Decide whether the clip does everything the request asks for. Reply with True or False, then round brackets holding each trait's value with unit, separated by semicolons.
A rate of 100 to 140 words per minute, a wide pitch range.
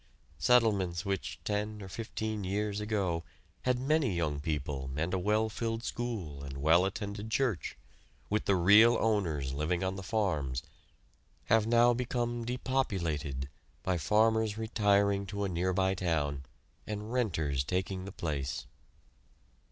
False (135 wpm; 4.9 semitones)